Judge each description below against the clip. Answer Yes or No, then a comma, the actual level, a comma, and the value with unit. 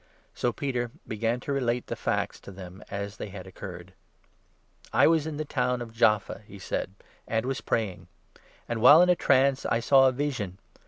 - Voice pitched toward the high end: No, low, 120 Hz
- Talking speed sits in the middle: No, fast, 215 wpm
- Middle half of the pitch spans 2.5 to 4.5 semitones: No, average, 5.0 semitones